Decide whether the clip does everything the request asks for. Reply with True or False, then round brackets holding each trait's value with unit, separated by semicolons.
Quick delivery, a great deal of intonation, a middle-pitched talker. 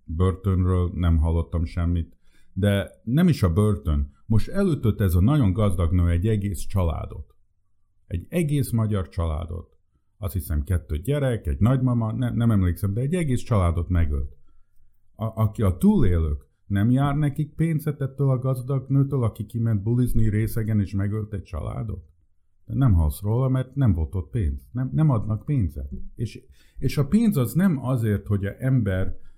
False (165 wpm; 6.0 semitones; 100 Hz)